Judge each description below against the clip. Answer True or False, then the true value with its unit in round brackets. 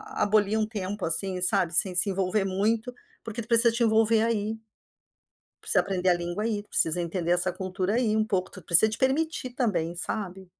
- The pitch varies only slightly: False (3.3 semitones)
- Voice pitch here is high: True (205 Hz)